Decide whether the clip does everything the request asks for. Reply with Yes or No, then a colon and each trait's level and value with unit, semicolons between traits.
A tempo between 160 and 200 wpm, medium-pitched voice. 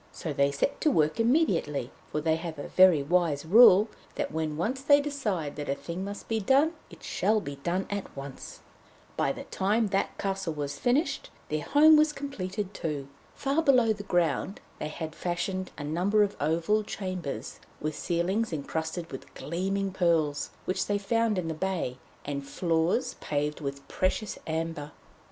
Yes: average, 175 wpm; medium, 180 Hz